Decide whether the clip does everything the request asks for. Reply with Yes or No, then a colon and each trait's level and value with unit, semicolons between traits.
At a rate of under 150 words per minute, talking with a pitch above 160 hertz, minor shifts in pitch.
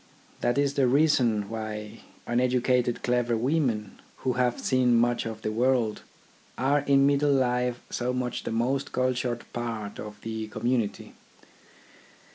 No: average, 140 wpm; low, 125 Hz; narrow, 2.3 semitones